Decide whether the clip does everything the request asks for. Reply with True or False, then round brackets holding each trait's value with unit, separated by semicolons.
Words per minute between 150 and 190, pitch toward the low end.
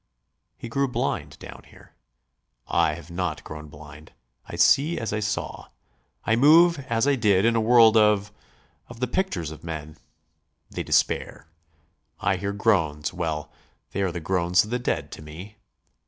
True (165 wpm; 100 Hz)